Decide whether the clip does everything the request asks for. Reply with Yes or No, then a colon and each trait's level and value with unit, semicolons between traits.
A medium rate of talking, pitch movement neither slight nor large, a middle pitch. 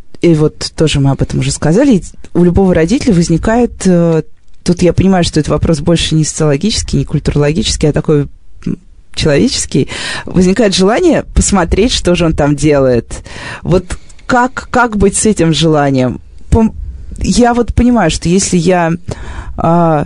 Yes: average, 140 wpm; average, 4.4 semitones; medium, 165 Hz